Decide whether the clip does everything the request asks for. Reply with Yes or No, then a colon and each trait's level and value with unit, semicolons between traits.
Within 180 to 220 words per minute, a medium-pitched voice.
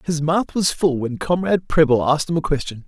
No: fast, 230 wpm; medium, 155 Hz